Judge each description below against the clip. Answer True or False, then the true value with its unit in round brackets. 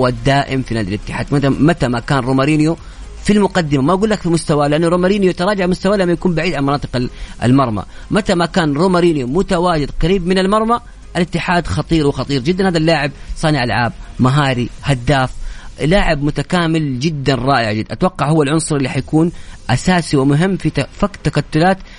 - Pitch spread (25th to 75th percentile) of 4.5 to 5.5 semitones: True (5.0 semitones)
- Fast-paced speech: True (160 wpm)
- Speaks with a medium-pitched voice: True (150 Hz)